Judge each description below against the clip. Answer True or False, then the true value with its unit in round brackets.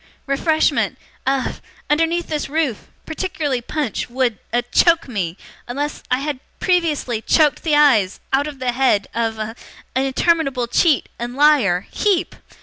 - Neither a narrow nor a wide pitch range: True (4.3 semitones)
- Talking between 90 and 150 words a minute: True (140 wpm)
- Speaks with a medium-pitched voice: False (275 Hz)